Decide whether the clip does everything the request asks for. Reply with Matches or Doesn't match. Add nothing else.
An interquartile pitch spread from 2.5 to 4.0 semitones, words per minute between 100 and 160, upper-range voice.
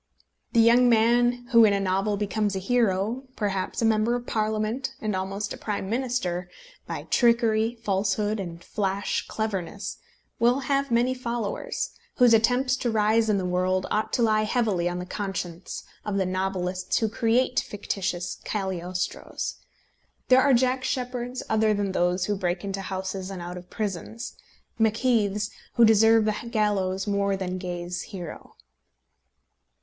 Matches